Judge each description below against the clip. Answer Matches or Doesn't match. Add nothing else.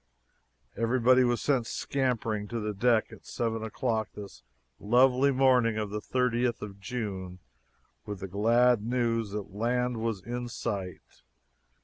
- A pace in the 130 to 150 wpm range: Matches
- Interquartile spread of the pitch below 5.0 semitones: Matches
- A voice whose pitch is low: Matches